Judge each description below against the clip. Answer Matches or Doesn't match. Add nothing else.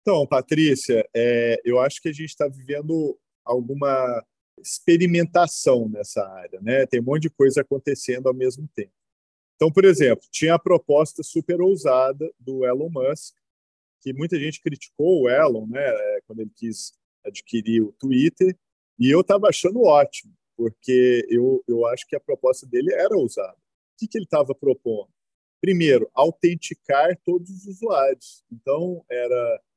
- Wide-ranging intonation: Matches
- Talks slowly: Doesn't match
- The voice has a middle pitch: Matches